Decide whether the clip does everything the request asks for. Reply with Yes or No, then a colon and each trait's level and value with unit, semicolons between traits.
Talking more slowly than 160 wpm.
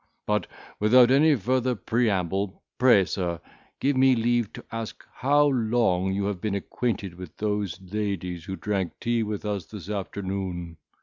Yes: average, 150 wpm